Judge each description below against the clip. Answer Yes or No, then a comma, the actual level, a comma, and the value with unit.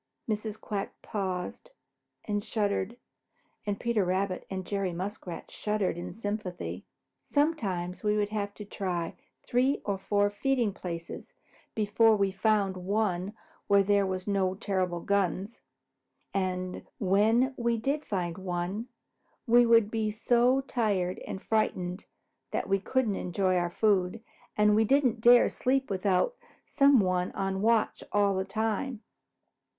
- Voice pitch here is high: Yes, high, 205 Hz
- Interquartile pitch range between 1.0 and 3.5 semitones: Yes, average, 3.0 semitones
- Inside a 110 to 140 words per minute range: Yes, slow, 135 wpm